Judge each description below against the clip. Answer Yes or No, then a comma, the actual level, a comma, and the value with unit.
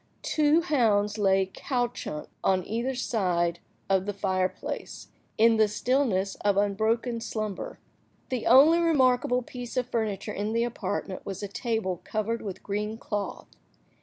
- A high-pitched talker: Yes, high, 215 Hz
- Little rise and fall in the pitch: No, average, 3.7 semitones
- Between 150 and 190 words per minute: No, slow, 135 wpm